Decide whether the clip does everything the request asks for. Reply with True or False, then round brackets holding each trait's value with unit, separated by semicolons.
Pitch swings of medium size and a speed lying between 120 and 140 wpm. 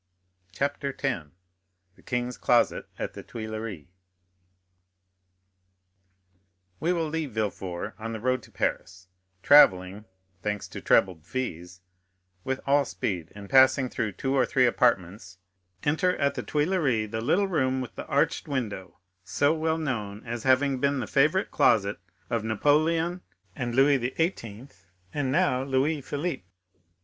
False (6.0 semitones; 135 wpm)